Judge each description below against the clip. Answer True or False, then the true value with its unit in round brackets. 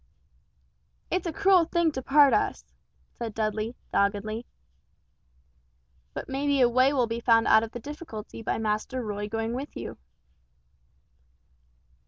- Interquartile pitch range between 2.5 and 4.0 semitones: False (4.5 semitones)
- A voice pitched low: False (240 Hz)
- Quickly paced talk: False (140 wpm)